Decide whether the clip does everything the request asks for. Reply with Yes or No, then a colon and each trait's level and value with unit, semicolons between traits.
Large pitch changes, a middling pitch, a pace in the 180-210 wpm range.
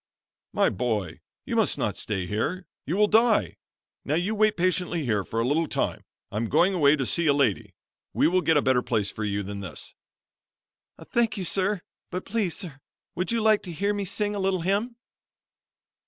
Yes: wide, 8.4 semitones; medium, 175 Hz; average, 195 wpm